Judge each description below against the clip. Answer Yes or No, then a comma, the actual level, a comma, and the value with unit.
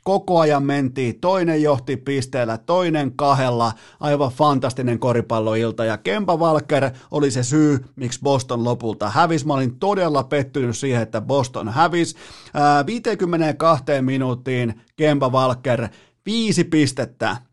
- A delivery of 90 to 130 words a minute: Yes, average, 120 wpm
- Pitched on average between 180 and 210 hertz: No, medium, 140 Hz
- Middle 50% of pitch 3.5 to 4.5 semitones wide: Yes, average, 4.0 semitones